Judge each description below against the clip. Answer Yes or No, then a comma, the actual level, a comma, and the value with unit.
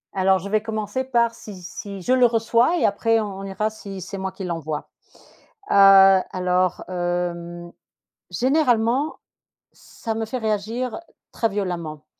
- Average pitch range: Yes, average, 3.7 semitones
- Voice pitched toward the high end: Yes, high, 200 Hz